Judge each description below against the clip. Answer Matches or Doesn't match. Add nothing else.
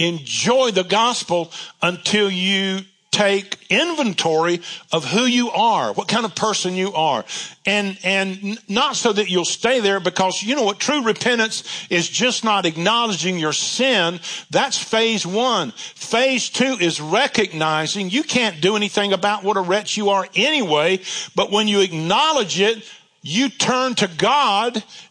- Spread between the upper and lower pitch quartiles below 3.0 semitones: Doesn't match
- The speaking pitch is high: Matches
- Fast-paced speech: Doesn't match